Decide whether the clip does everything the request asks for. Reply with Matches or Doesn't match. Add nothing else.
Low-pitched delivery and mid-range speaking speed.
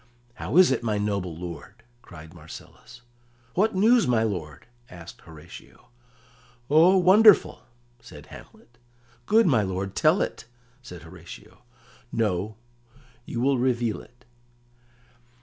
Doesn't match